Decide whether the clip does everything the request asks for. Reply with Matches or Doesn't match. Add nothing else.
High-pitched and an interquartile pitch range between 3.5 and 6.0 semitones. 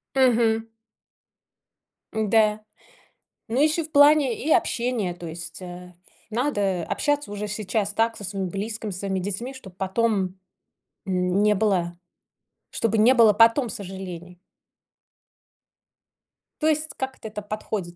Matches